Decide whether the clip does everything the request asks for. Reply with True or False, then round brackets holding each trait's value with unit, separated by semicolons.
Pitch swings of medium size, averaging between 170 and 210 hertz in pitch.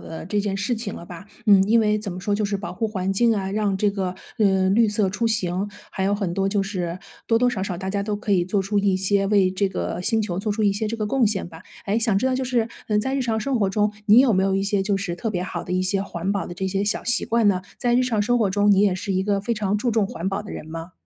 False (2.1 semitones; 200 Hz)